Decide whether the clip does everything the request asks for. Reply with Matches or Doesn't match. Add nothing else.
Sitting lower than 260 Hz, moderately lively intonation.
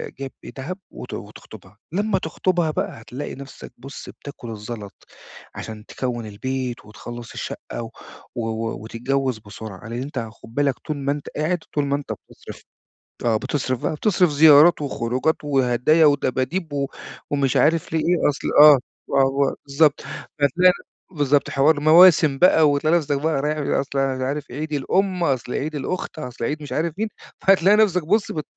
Matches